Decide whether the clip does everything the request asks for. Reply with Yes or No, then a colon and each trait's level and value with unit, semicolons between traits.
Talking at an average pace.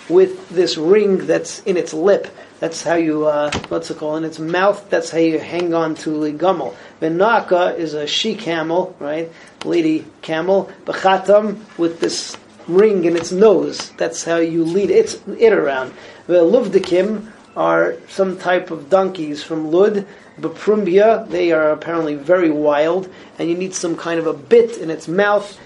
Yes: average, 170 wpm